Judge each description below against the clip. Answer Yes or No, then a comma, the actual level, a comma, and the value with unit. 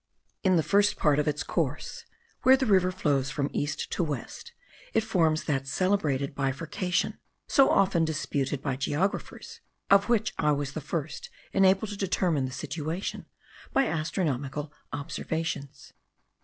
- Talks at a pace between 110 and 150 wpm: Yes, average, 140 wpm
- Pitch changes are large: No, average, 4.9 semitones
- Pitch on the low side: No, medium, 155 Hz